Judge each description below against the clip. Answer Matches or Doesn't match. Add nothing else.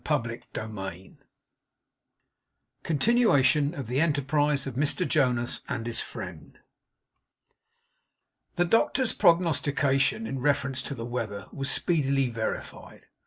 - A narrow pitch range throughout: Doesn't match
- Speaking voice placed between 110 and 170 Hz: Matches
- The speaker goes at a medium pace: Doesn't match